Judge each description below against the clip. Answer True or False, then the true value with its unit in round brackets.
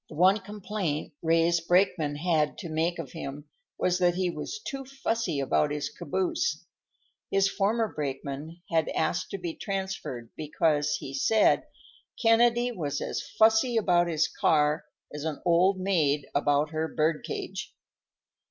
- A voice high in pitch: False (170 Hz)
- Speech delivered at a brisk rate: False (145 wpm)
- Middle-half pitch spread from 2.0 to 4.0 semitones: False (4.6 semitones)